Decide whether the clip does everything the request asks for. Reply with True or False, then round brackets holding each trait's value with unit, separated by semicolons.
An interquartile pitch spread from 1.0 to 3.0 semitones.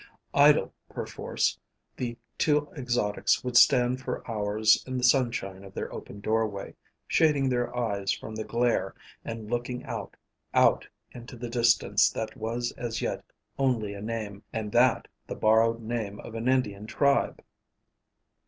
True (2.4 semitones)